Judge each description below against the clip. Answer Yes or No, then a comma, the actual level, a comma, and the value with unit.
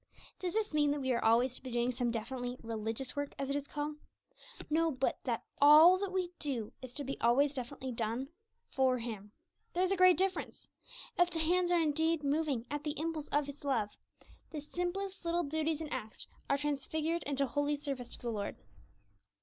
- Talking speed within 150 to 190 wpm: No, average, 200 wpm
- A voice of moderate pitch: No, very high, 285 Hz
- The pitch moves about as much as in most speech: Yes, average, 4.2 semitones